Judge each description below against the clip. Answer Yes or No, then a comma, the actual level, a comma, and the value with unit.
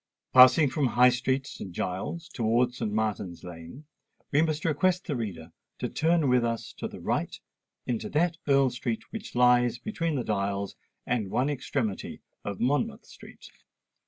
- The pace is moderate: Yes, average, 160 wpm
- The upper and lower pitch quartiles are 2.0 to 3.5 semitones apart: No, average, 5.3 semitones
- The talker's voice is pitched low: Yes, low, 125 Hz